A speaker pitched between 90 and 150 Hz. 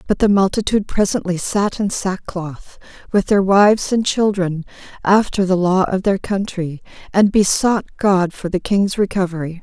No: high, 190 Hz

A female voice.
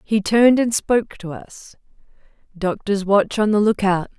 Yes: female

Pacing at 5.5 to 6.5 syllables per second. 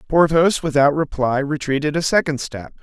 No: 5.0 syllables/s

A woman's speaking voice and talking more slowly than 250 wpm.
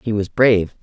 Yes: female; fast, 215 wpm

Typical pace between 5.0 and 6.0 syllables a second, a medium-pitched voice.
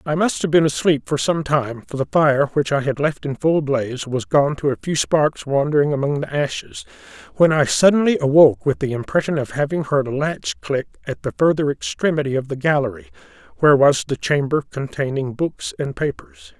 Yes: 5.4 syllables/s; medium, 145 Hz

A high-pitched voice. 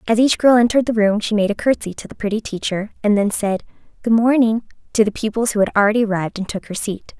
Yes: high, 215 Hz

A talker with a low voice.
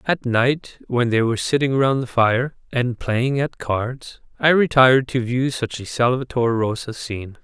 Yes: low, 125 Hz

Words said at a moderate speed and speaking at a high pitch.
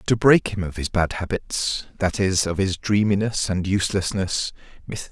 No: average, 150 wpm; very low, 95 Hz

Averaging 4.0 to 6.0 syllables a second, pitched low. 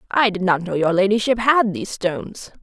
No: 5.6 syllables/s; high, 200 Hz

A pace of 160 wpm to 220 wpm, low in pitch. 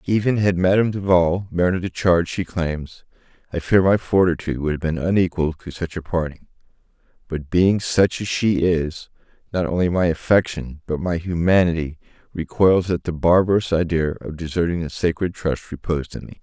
Yes: average, 170 wpm; very low, 85 Hz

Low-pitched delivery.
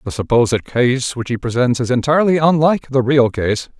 Yes: low, 130 Hz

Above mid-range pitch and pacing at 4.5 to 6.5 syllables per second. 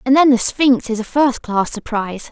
Yes: high, 245 Hz; 5.0 syllables/s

